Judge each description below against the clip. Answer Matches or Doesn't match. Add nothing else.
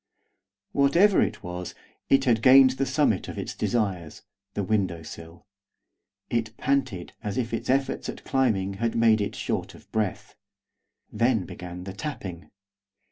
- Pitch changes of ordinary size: Doesn't match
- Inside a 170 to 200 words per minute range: Doesn't match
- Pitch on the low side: Matches